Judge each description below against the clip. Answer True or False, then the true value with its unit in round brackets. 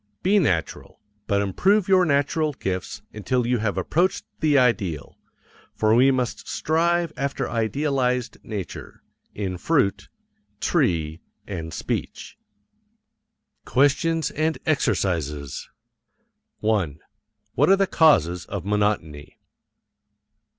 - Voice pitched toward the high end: False (115 Hz)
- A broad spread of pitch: True (8.6 semitones)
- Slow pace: True (100 wpm)